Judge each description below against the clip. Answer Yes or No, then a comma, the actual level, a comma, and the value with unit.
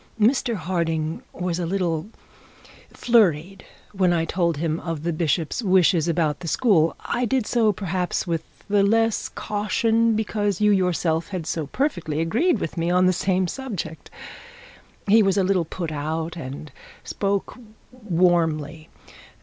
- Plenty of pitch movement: No, average, 4.1 semitones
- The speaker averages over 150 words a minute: No, average, 140 wpm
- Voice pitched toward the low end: No, medium, 180 Hz